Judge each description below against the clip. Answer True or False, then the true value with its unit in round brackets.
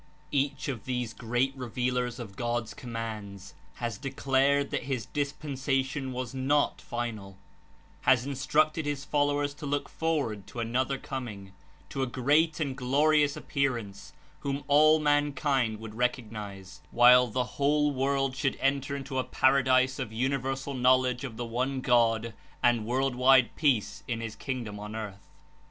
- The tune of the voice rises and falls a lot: False (3.0 semitones)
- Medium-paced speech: True (155 wpm)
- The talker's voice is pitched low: True (130 Hz)